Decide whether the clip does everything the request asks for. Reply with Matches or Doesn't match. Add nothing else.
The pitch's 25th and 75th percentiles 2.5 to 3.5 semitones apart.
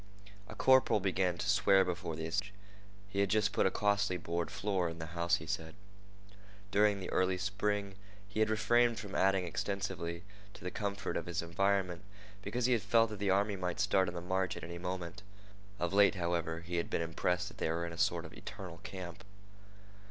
Matches